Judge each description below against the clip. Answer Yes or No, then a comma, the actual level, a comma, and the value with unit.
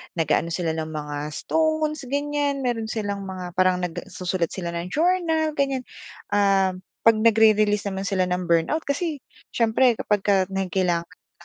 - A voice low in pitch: No, high, 205 Hz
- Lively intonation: Yes, wide, 7.3 semitones